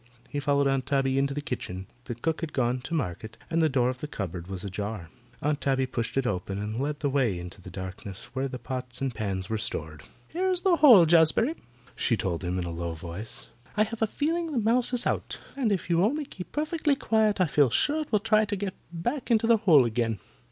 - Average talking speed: No, fast, 230 wpm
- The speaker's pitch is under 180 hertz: Yes, low, 135 Hz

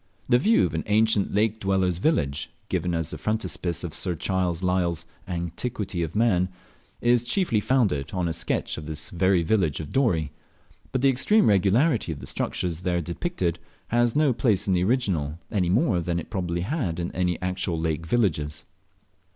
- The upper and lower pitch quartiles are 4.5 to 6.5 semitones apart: Yes, average, 4.8 semitones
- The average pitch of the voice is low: Yes, very low, 90 Hz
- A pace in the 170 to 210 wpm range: Yes, average, 175 wpm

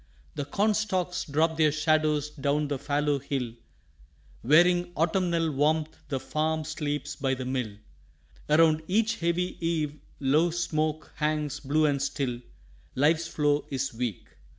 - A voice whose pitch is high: No, medium, 150 Hz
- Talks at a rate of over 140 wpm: No, slow, 135 wpm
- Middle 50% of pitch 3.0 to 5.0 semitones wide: No, narrow, 2.4 semitones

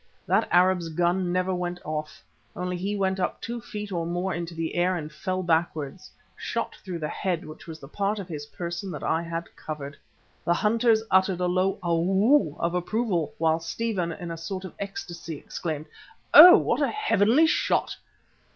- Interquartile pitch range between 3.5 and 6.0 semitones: No, average, 2.7 semitones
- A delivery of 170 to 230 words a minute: Yes, average, 180 wpm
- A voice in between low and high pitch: Yes, medium, 180 Hz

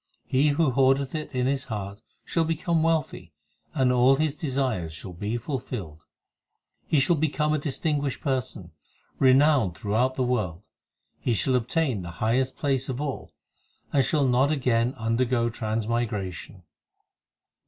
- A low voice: Yes, low, 130 Hz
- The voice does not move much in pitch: No, average, 4.3 semitones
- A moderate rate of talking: Yes, average, 145 wpm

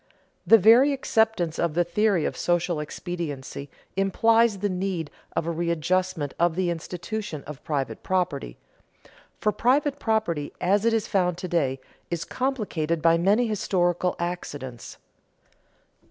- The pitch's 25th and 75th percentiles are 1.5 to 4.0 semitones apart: No, average, 4.4 semitones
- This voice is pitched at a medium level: Yes, medium, 175 Hz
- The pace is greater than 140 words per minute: No, slow, 135 wpm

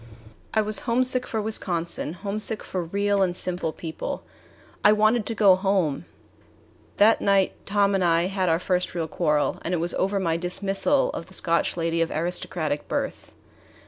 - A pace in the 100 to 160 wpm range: No, average, 170 wpm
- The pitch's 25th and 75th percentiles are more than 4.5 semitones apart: No, average, 3.4 semitones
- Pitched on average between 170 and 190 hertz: Yes, medium, 185 Hz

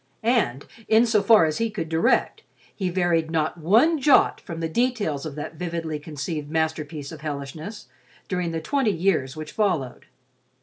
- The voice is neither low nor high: Yes, medium, 165 Hz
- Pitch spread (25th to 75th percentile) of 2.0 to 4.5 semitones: No, average, 5.2 semitones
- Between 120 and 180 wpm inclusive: Yes, average, 165 wpm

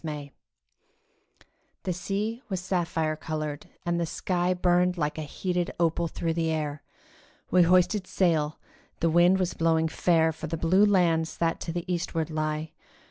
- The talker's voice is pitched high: No, medium, 170 Hz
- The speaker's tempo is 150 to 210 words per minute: Yes, average, 155 wpm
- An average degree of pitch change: No, narrow, 2.1 semitones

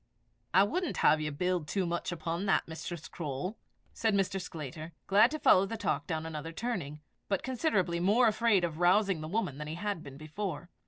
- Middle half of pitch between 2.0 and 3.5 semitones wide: No, average, 4.5 semitones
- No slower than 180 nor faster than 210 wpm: Yes, average, 195 wpm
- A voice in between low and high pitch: Yes, medium, 175 Hz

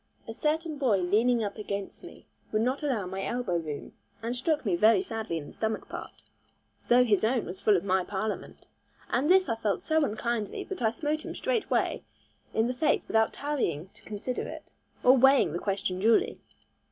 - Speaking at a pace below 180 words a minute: No, average, 190 wpm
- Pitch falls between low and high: No, high, 225 Hz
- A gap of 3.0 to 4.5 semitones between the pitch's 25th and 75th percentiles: No, average, 4.9 semitones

